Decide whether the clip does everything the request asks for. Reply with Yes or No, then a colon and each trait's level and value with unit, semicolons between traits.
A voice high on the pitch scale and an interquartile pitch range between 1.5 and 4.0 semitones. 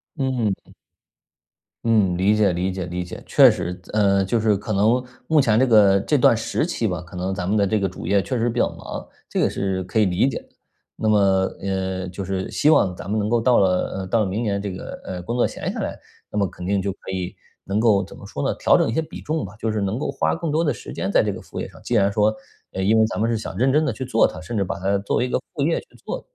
No: low, 105 Hz; average, 3.6 semitones